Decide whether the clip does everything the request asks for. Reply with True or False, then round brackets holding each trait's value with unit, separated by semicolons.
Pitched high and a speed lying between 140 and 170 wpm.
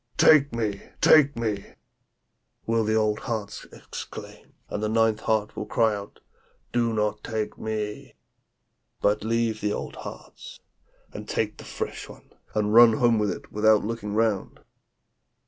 False (110 Hz; 150 wpm)